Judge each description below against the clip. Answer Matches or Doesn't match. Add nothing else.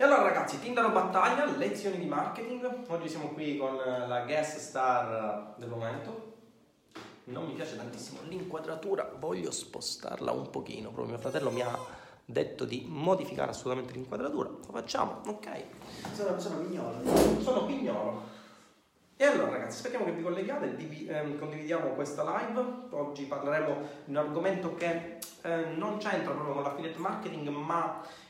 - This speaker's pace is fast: Doesn't match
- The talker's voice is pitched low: Doesn't match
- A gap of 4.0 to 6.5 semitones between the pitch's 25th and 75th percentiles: Matches